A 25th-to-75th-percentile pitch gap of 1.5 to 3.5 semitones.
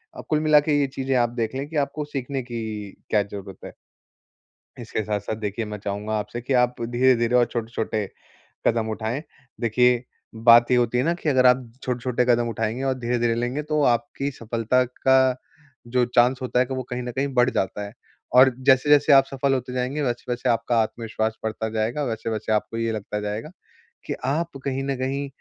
Yes: average, 2.8 semitones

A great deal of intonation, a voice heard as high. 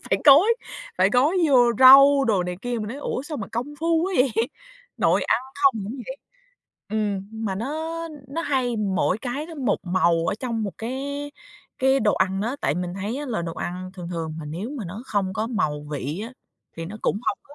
Yes: wide, 6.4 semitones; high, 225 Hz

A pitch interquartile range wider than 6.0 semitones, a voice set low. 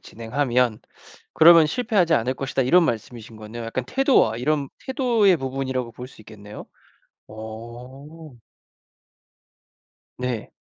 No: wide, 5.7 semitones; low, 130 Hz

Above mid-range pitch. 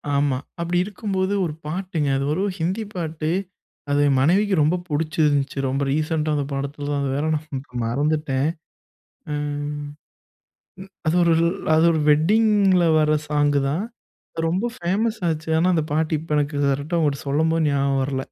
No: medium, 155 Hz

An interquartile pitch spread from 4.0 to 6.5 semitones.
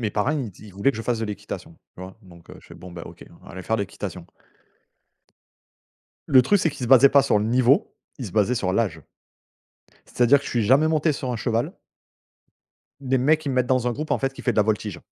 Yes: average, 4.6 semitones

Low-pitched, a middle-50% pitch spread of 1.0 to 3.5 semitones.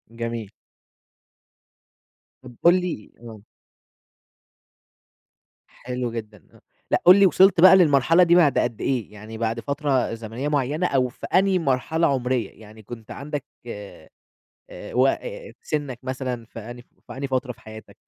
No: low, 130 Hz; average, 4.6 semitones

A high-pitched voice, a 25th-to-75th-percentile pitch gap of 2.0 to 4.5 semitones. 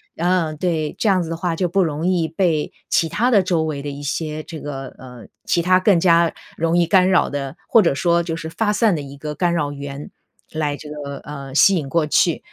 No: medium, 165 Hz; average, 3.2 semitones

